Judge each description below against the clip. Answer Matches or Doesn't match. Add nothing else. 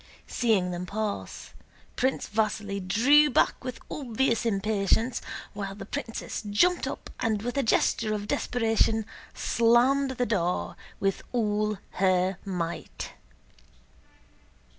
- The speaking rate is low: Matches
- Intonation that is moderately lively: Matches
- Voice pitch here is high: Matches